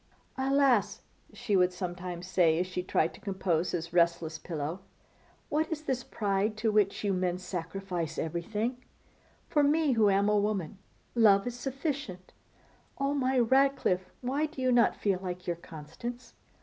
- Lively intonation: Yes, wide, 5.9 semitones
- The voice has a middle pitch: No, high, 200 Hz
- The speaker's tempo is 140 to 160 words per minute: Yes, average, 155 wpm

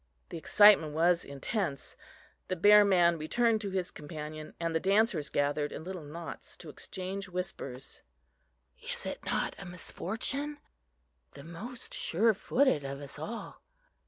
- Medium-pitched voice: Yes, medium, 175 Hz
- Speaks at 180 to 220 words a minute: No, slow, 135 wpm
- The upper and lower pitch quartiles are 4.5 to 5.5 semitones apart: Yes, average, 5.2 semitones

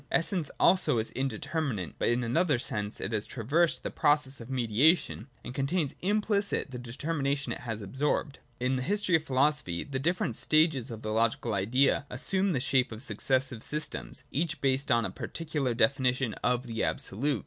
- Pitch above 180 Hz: No, low, 135 Hz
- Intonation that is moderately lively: Yes, average, 4.5 semitones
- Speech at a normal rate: Yes, average, 175 wpm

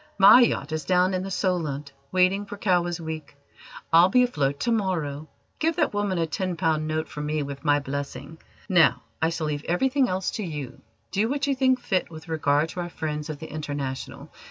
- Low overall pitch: No, medium, 165 Hz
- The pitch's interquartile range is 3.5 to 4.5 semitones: Yes, average, 4.2 semitones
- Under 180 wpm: No, fast, 205 wpm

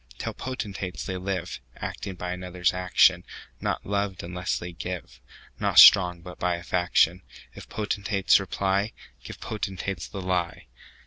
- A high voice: No, very low, 90 Hz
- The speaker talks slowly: Yes, slow, 115 wpm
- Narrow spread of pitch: Yes, narrow, 1.7 semitones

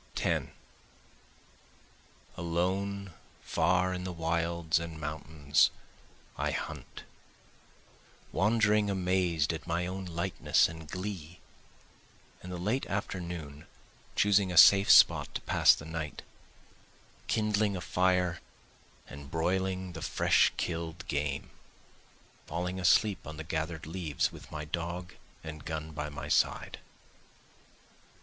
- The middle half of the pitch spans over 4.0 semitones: No, average, 2.9 semitones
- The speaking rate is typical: No, slow, 115 wpm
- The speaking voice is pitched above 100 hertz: No, very low, 85 Hz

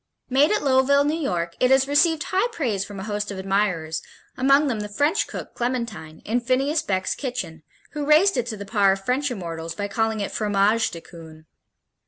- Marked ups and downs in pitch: Yes, wide, 6.1 semitones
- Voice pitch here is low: No, high, 225 Hz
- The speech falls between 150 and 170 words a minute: No, average, 200 wpm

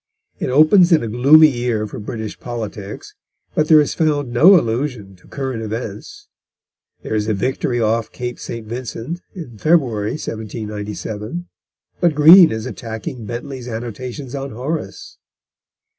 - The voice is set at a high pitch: No, low, 120 Hz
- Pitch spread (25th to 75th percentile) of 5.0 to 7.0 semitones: Yes, wide, 5.4 semitones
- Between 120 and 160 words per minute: Yes, average, 140 wpm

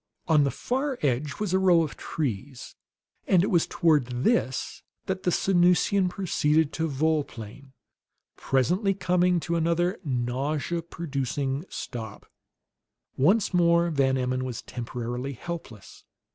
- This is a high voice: No, medium, 155 Hz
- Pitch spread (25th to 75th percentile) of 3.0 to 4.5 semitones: No, average, 5.1 semitones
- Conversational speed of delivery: No, slow, 125 wpm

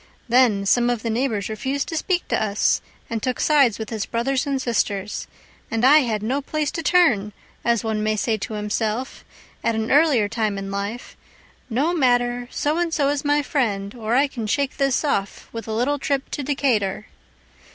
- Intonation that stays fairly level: No, average, 4.5 semitones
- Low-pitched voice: No, high, 240 Hz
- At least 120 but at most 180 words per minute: No, average, 195 wpm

